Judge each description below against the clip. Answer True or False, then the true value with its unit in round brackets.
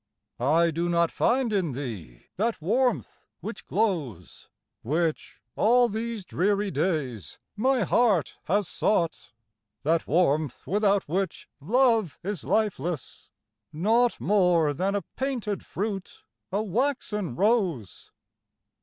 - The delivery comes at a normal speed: False (110 wpm)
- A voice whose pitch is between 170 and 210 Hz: True (190 Hz)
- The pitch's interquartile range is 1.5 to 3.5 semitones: False (5.5 semitones)